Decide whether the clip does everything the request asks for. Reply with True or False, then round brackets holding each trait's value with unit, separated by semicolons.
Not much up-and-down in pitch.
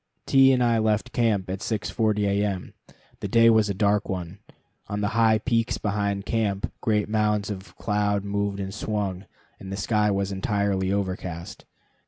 True (1.8 semitones)